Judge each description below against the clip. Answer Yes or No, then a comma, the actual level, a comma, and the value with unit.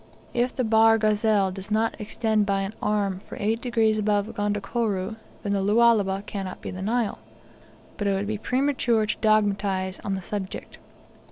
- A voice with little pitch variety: Yes, narrow, 2.1 semitones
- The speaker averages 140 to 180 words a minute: Yes, average, 170 wpm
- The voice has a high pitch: Yes, high, 210 Hz